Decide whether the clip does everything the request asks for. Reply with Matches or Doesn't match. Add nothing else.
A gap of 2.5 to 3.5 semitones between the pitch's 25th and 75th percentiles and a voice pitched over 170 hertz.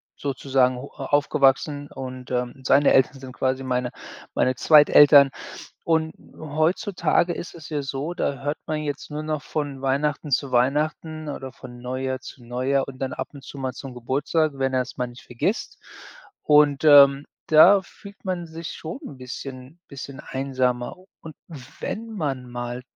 Doesn't match